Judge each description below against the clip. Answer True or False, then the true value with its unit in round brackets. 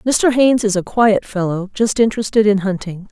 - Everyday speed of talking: True (190 wpm)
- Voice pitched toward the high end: True (210 Hz)